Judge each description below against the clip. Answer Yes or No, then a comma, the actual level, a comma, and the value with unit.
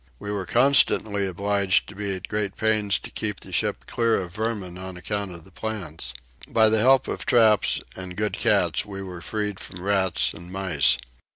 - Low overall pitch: Yes, low, 100 Hz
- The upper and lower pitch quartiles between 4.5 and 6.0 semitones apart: No, average, 2.8 semitones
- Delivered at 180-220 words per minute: Yes, average, 190 wpm